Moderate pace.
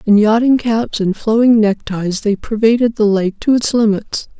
Yes: average, 180 wpm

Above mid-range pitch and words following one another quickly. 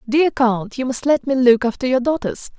Yes: very high, 255 Hz; fast, 230 wpm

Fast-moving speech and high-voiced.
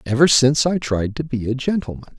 No: fast, 220 wpm; low, 130 Hz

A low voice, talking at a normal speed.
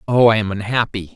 No: low, 110 Hz; fast, 210 wpm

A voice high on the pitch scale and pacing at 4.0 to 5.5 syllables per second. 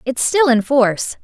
Yes: very high, 255 Hz; 4.7 syllables/s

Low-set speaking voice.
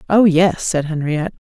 No: medium, 170 Hz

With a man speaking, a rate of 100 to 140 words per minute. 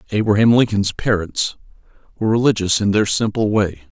Yes: male; slow, 135 wpm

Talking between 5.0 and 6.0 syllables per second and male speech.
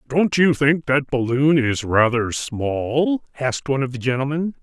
No: 4.5 syllables/s; male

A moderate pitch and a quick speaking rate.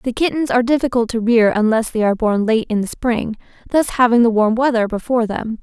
No: high, 230 Hz; fast, 225 wpm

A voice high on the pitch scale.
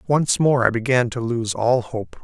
No: low, 120 Hz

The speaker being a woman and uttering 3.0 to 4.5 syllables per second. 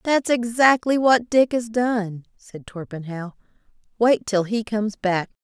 Yes: female; 4.0 syllables/s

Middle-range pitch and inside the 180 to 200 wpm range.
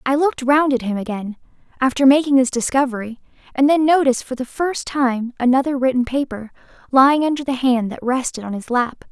No: very high, 260 Hz; average, 190 wpm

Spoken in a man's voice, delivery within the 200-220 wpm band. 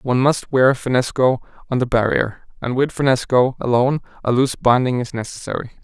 No: male; average, 165 wpm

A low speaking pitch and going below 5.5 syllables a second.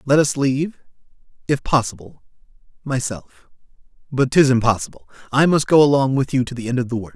No: low, 130 Hz; 5.9 syllables/s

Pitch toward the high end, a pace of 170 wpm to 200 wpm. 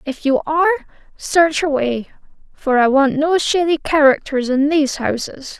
No: very high, 295 Hz; average, 150 wpm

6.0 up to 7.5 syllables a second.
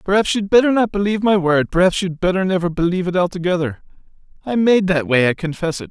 Yes: 6.5 syllables/s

